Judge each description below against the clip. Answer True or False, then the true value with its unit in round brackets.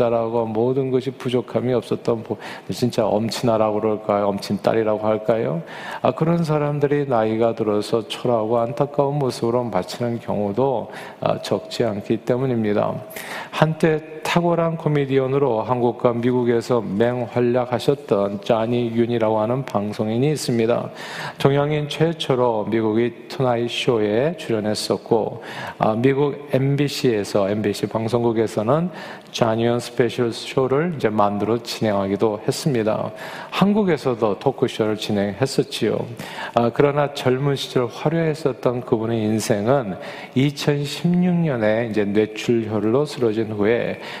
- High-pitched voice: False (120 Hz)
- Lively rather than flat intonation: False (4.3 semitones)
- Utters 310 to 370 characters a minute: False (295 characters per minute)